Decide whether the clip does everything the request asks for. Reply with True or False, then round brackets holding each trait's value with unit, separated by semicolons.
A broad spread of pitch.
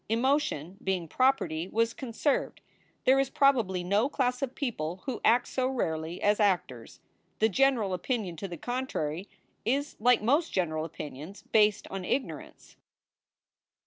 True (6.6 semitones)